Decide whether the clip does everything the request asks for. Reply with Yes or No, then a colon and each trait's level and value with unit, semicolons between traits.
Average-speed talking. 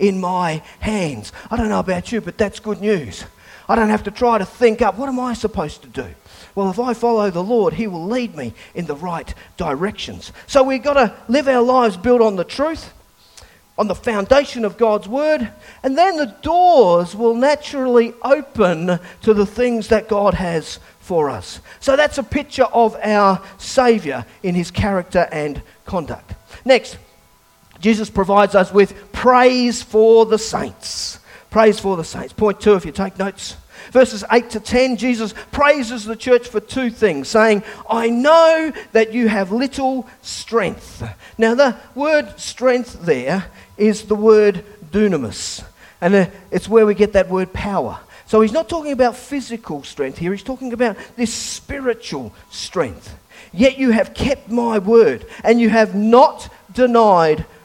Yes: average, 170 wpm